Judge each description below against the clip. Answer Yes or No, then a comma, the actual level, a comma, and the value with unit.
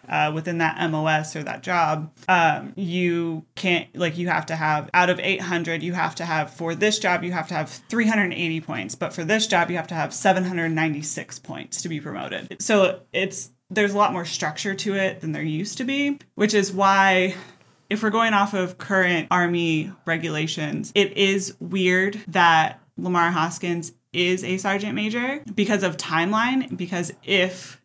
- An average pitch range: Yes, average, 3.3 semitones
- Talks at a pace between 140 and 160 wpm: No, average, 180 wpm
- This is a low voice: No, medium, 180 Hz